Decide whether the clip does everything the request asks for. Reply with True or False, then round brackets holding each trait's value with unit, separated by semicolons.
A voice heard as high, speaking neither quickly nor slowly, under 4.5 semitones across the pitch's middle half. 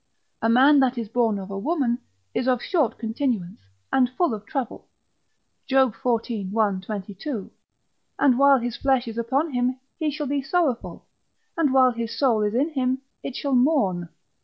True (250 Hz; 170 wpm; 3.7 semitones)